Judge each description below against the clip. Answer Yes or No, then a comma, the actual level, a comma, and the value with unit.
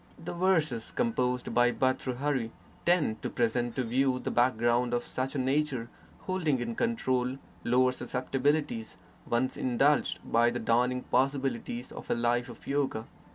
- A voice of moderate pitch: No, low, 125 Hz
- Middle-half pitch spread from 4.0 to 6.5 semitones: No, narrow, 2.4 semitones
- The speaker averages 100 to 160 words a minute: Yes, average, 150 wpm